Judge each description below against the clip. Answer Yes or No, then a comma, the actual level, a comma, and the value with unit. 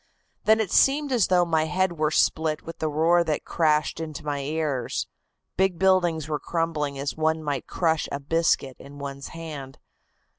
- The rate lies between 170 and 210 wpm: Yes, average, 175 wpm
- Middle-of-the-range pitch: Yes, medium, 160 Hz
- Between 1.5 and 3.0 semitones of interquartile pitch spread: Yes, average, 2.7 semitones